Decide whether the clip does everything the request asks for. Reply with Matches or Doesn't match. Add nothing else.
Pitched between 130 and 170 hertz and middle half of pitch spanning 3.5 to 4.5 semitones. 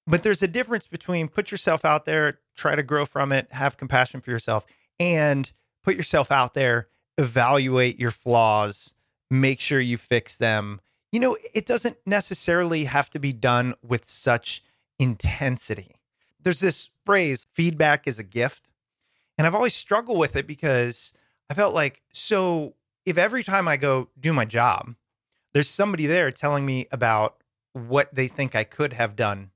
Doesn't match